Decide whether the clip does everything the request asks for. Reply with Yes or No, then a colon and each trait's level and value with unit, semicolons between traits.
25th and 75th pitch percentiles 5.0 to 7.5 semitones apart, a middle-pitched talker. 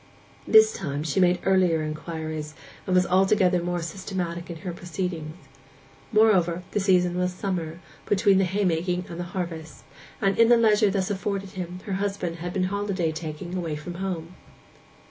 No: narrow, 2.5 semitones; medium, 180 Hz